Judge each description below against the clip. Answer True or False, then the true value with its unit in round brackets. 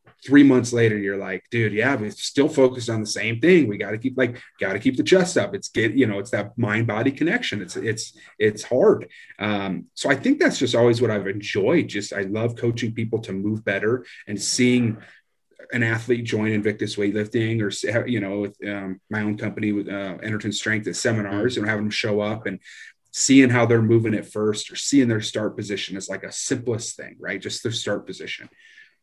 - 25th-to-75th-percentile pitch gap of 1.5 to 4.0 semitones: True (2.9 semitones)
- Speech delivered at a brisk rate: True (215 wpm)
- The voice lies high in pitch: False (110 Hz)